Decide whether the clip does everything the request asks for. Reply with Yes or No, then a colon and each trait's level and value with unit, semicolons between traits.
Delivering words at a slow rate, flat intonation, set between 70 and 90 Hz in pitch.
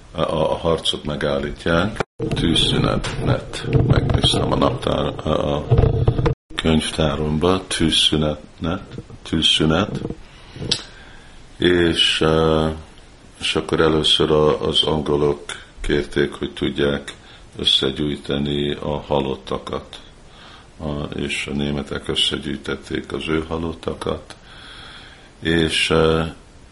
Yes: slow, 70 wpm; narrow, 1.9 semitones; very low, 80 Hz